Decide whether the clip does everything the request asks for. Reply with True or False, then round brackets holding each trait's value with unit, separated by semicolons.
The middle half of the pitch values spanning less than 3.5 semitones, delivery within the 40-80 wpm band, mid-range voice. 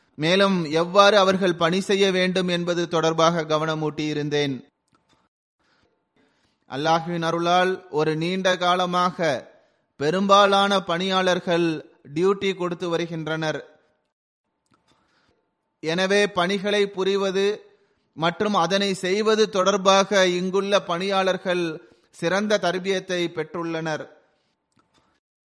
True (2.9 semitones; 75 wpm; 180 Hz)